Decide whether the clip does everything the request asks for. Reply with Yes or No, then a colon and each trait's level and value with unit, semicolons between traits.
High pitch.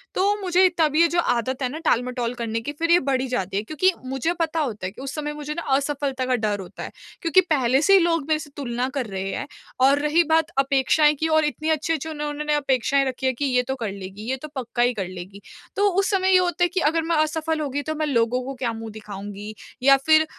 Yes: very high, 275 Hz